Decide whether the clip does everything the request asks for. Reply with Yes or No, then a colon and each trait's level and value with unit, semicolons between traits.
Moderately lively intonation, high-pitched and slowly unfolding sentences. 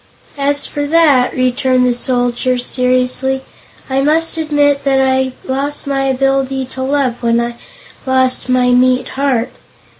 No: narrow, 1.6 semitones; very high, 260 Hz; slow, 130 wpm